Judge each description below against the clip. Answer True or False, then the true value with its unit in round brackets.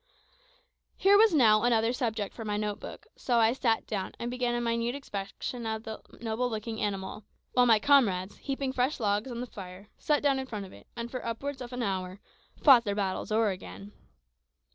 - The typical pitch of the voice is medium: False (230 Hz)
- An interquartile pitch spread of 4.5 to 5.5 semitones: False (3.4 semitones)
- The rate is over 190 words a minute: True (200 wpm)